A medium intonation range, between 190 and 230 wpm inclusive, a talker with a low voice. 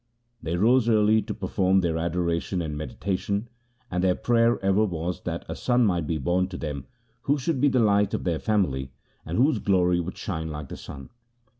Yes: average, 4.5 semitones; average, 195 wpm; very low, 95 Hz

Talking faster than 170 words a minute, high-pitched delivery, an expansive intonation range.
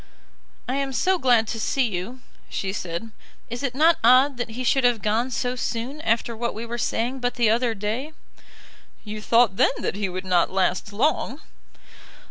No: average, 185 wpm; high, 235 Hz; average, 3.1 semitones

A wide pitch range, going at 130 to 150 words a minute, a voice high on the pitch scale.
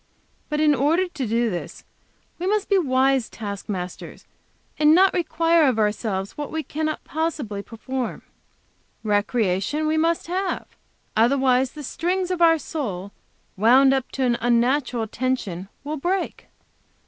Yes: wide, 6.0 semitones; average, 140 wpm; very high, 270 Hz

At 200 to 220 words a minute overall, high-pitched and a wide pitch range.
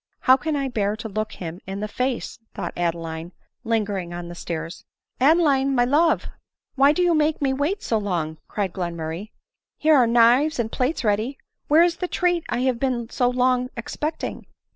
Yes: fast, 205 wpm; high, 245 Hz; wide, 6.2 semitones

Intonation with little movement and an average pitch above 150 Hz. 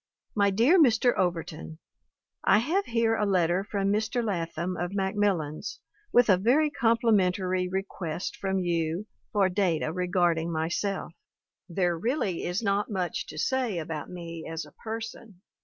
No: average, 4.2 semitones; high, 190 Hz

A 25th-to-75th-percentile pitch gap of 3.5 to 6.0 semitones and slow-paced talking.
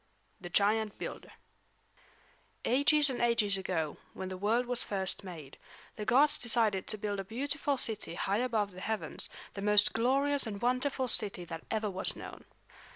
No: average, 4.2 semitones; average, 160 wpm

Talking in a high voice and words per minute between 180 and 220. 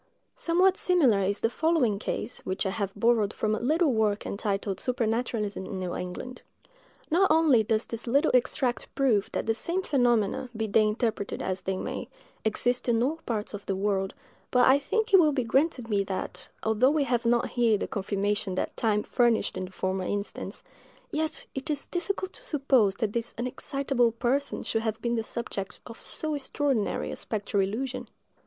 Yes: high, 230 Hz; average, 185 wpm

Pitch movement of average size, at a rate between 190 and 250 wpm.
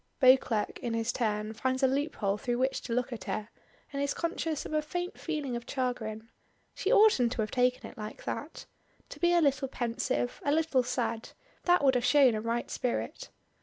Yes: average, 3.7 semitones; fast, 205 wpm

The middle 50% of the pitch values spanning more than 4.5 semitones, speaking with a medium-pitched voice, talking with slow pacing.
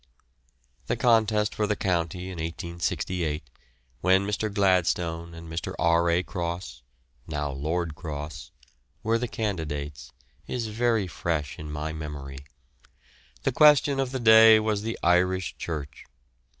No: average, 5.1 semitones; very low, 85 Hz; slow, 130 wpm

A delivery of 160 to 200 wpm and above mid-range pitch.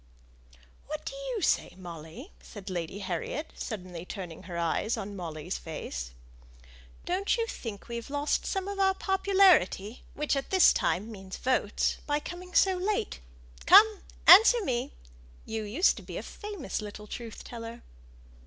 No: average, 150 wpm; high, 235 Hz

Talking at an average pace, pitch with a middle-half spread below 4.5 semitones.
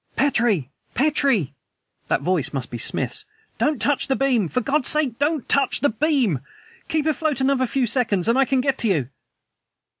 No: average, 175 wpm; average, 5.3 semitones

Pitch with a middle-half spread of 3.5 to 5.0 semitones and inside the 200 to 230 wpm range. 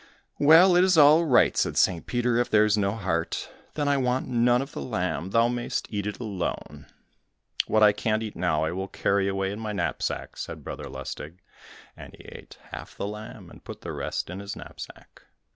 Yes: average, 4.1 semitones; fast, 205 wpm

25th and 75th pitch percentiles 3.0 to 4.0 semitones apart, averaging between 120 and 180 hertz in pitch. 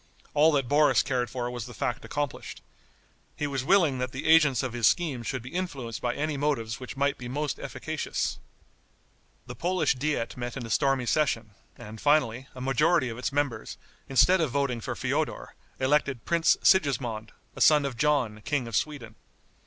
Yes: average, 3.5 semitones; low, 135 Hz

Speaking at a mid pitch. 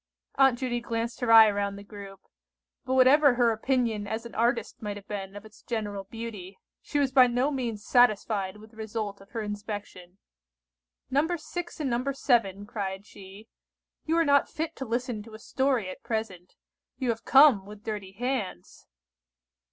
No: high, 225 Hz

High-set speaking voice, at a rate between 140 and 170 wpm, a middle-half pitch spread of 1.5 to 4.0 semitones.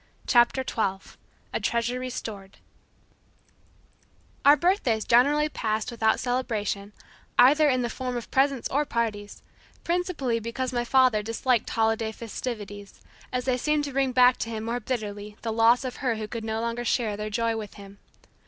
Yes: high, 235 Hz; average, 160 wpm; average, 2.7 semitones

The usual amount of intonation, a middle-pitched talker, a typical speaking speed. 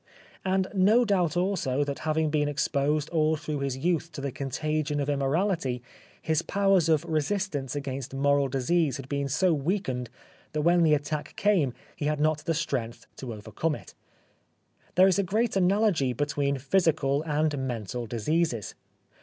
Yes: average, 3.8 semitones; medium, 150 Hz; average, 165 wpm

